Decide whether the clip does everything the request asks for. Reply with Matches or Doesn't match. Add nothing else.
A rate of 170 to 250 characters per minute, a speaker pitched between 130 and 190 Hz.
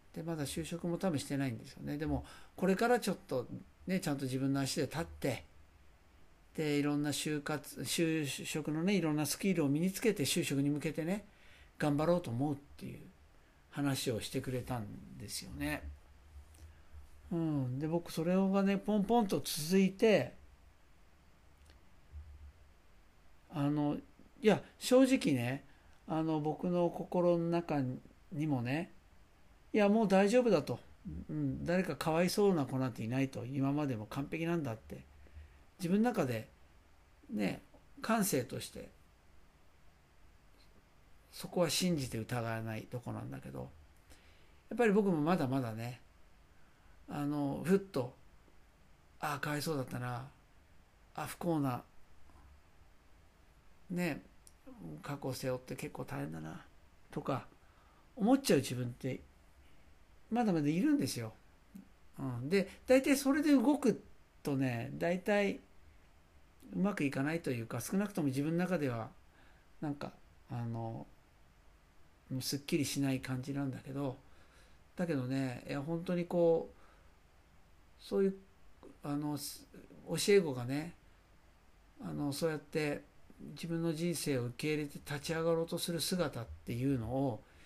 Matches